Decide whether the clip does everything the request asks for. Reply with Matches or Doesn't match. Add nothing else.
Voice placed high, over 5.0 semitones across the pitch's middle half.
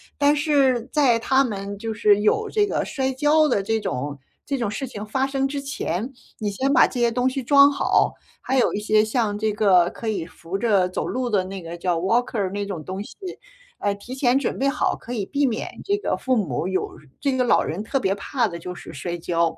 Matches